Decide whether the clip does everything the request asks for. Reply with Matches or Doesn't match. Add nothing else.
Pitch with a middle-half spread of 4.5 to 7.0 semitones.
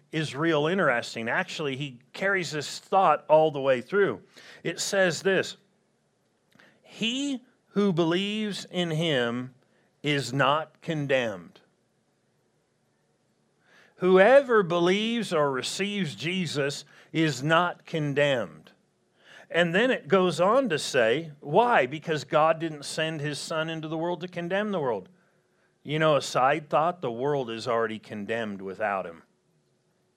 Matches